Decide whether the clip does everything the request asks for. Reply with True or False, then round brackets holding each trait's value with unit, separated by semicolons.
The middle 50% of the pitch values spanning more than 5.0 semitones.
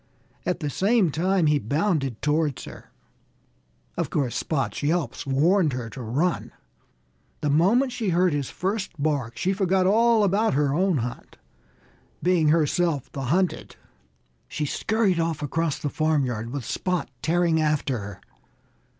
False (4.6 semitones)